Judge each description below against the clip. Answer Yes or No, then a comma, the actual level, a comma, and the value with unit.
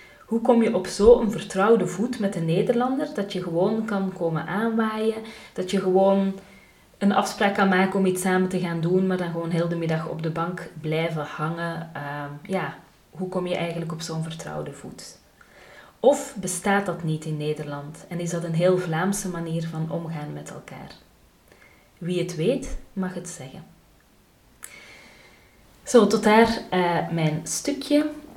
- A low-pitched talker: No, medium, 185 Hz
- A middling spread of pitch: Yes, average, 3.4 semitones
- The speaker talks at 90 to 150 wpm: No, average, 165 wpm